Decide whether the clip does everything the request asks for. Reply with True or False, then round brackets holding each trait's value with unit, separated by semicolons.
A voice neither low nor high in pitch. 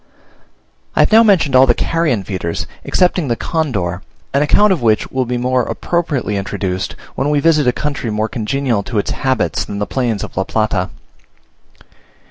False (125 Hz)